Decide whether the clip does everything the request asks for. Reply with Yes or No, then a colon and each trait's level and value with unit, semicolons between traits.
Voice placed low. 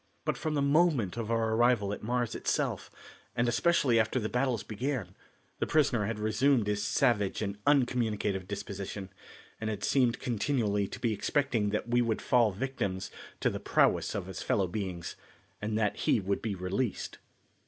Yes: low, 110 Hz